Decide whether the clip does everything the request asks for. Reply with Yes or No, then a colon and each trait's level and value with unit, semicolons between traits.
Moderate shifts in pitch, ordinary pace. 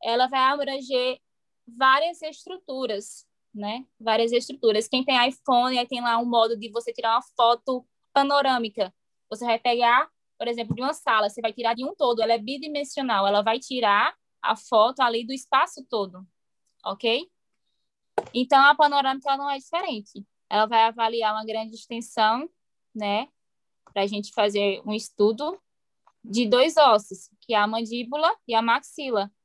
Yes: average, 3.5 semitones; average, 160 wpm